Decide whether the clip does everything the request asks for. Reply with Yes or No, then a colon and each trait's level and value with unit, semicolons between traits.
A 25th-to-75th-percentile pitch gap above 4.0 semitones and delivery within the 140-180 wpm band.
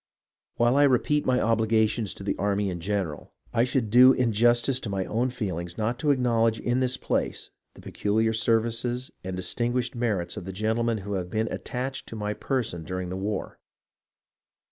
No: average, 3.3 semitones; average, 175 wpm